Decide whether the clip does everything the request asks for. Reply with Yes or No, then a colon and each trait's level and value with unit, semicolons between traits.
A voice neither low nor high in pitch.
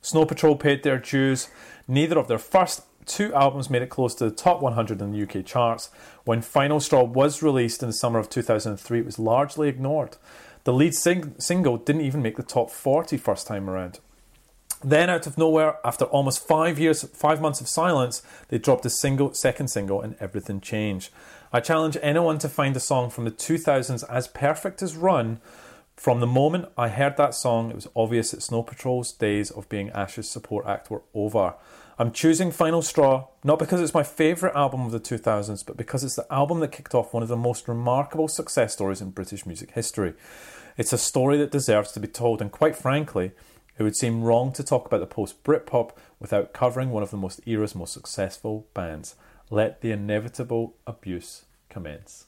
No: low, 125 Hz